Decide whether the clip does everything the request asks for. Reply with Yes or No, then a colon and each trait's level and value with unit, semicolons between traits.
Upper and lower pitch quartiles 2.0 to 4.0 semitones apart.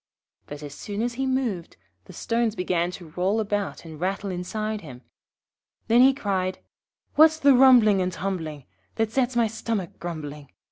No: average, 5.0 semitones